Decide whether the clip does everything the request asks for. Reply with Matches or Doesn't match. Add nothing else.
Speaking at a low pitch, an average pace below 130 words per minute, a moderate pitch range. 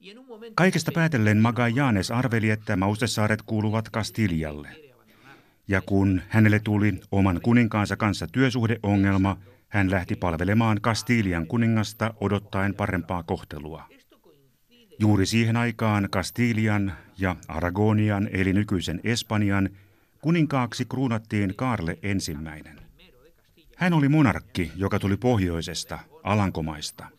Matches